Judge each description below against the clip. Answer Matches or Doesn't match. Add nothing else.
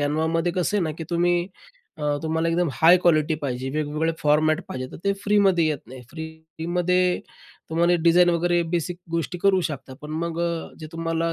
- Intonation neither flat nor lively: Doesn't match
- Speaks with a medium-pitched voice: Matches